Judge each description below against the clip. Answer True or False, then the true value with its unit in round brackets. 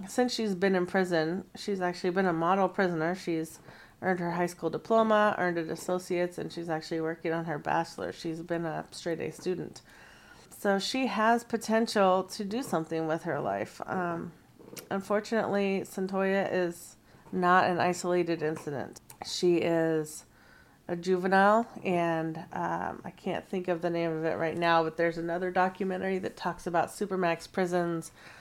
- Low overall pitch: False (180 Hz)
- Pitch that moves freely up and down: False (2.7 semitones)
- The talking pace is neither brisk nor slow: True (160 wpm)